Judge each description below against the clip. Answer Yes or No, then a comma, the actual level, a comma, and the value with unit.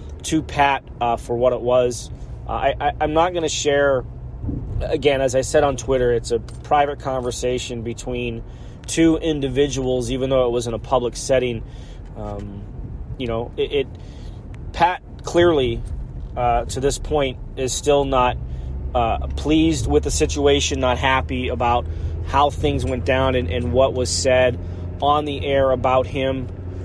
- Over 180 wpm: No, average, 160 wpm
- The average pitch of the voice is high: No, low, 125 Hz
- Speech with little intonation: No, average, 3.1 semitones